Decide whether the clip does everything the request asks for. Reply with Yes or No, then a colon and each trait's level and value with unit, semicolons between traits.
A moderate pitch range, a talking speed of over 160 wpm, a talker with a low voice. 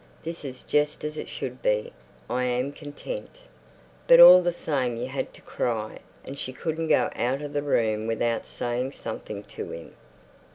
Yes: average, 4.2 semitones; average, 175 wpm; low, 130 Hz